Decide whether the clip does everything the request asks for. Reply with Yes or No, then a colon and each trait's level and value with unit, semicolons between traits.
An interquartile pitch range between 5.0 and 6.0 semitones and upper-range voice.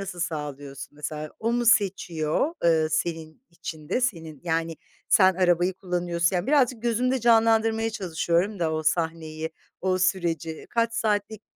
No: wide, 5.4 semitones; medium, 175 Hz